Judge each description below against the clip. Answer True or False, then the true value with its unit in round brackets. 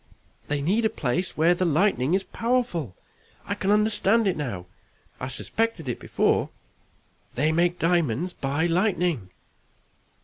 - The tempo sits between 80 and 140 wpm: True (135 wpm)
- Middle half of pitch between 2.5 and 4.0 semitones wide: False (5.6 semitones)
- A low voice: False (175 Hz)